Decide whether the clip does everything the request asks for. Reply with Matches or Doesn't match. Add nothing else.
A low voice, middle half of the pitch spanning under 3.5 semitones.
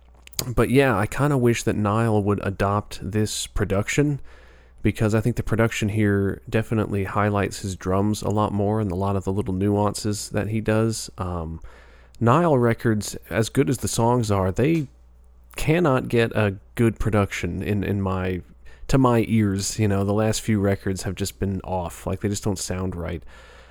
Matches